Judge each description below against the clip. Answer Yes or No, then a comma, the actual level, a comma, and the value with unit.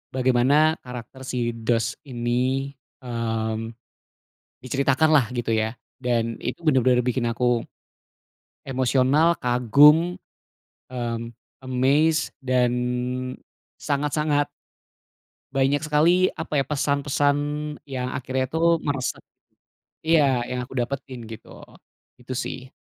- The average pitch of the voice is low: Yes, low, 130 Hz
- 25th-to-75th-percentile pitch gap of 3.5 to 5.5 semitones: No, average, 2.8 semitones